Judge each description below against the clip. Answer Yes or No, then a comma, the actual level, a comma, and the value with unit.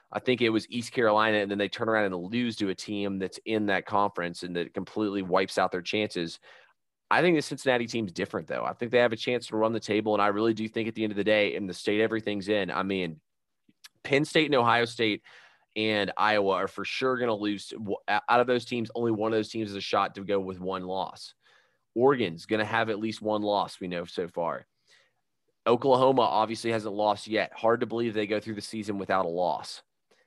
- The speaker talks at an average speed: No, fast, 235 wpm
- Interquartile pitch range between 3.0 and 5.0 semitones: No, narrow, 2.4 semitones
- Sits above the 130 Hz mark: No, low, 105 Hz